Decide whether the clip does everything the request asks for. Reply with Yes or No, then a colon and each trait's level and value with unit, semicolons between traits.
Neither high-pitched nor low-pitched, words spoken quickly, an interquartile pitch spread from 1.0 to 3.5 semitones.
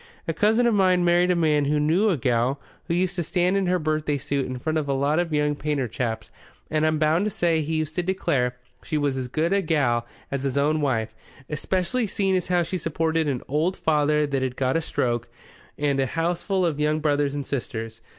No: medium, 155 Hz; fast, 230 wpm; average, 3.9 semitones